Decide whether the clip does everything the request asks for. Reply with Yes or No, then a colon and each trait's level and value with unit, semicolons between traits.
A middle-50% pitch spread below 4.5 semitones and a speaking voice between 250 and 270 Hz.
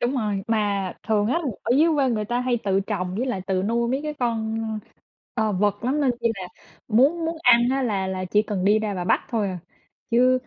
No: average, 3.8 semitones; high, 220 Hz